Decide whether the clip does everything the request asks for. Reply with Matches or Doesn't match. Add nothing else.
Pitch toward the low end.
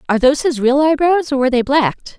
Doesn't match